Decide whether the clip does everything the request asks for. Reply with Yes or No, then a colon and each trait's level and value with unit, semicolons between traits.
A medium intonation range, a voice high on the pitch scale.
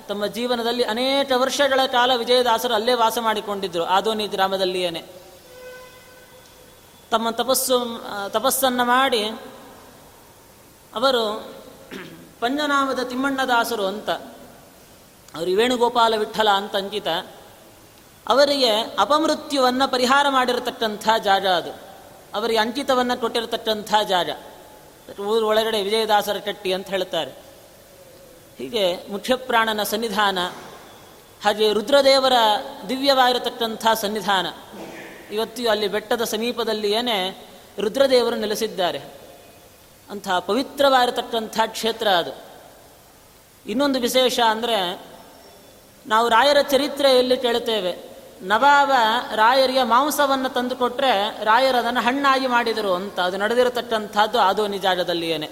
Yes: average, 3.6 semitones; high, 230 Hz